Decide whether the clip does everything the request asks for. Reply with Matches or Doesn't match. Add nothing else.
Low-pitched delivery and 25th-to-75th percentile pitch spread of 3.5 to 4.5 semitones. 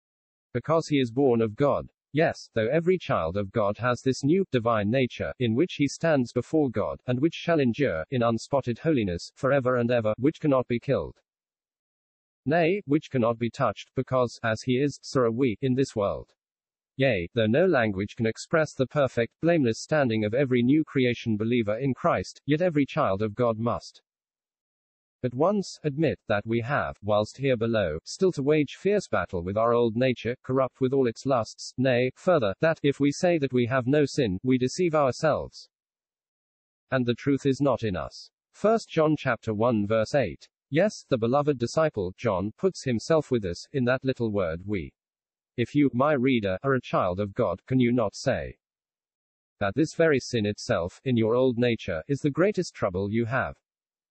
Matches